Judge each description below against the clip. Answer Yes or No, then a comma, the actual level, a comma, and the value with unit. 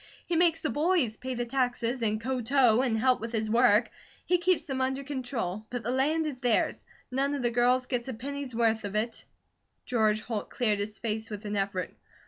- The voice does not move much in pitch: No, average, 3.4 semitones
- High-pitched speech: Yes, high, 245 Hz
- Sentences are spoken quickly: Yes, fast, 210 wpm